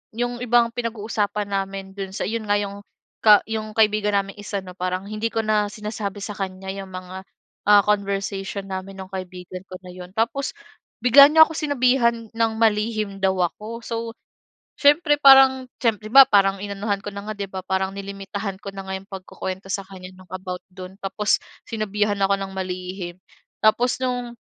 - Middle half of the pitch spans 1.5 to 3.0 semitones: Yes, average, 2.7 semitones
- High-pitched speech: Yes, high, 200 Hz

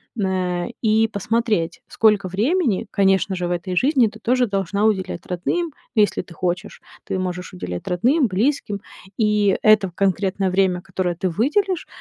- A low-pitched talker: No, high, 195 Hz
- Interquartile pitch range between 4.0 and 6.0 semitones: No, average, 3.5 semitones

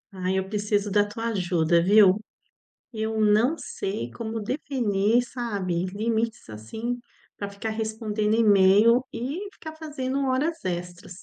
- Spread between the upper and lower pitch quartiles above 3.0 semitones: Yes, average, 3.4 semitones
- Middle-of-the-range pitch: No, high, 215 Hz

